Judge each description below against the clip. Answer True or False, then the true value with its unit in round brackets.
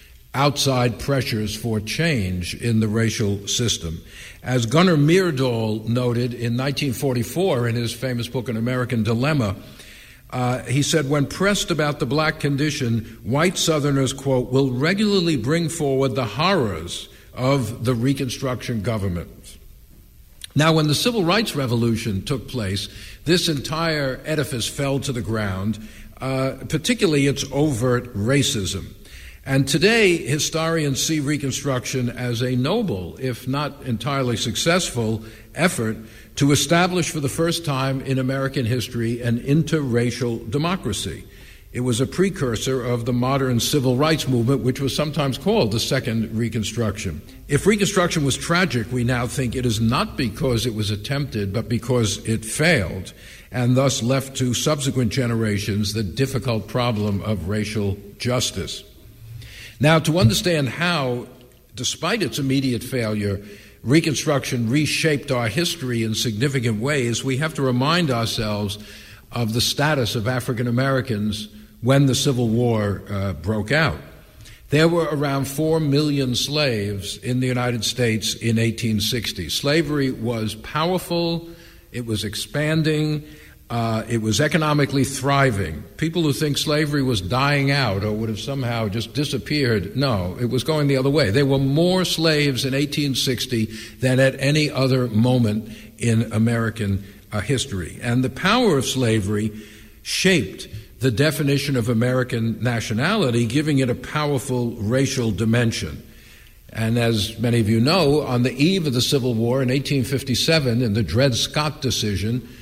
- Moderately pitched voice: False (125 Hz)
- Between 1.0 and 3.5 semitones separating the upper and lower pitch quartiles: False (4.2 semitones)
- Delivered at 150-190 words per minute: False (140 wpm)